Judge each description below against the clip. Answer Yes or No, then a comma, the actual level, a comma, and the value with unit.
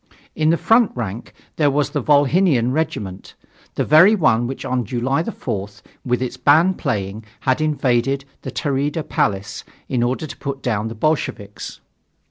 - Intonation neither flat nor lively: Yes, average, 4.7 semitones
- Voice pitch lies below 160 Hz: Yes, low, 135 Hz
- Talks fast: No, average, 155 wpm